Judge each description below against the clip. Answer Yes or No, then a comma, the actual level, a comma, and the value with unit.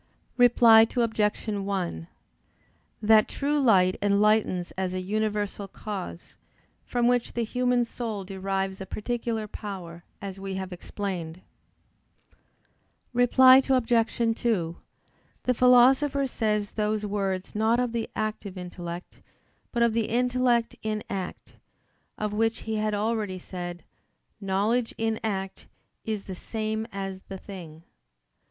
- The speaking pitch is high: Yes, high, 215 Hz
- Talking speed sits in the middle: No, slow, 120 wpm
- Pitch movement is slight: No, average, 3.3 semitones